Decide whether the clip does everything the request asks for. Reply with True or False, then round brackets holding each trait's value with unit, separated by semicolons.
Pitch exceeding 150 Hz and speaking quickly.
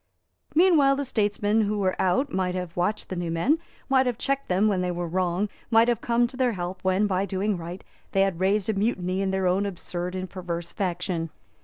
True (190 Hz; 215 wpm)